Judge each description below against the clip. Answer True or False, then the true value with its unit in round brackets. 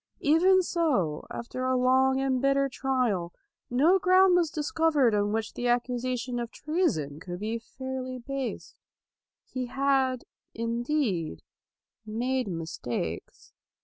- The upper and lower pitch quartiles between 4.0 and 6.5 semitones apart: False (3.4 semitones)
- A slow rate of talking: True (115 wpm)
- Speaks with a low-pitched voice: False (255 Hz)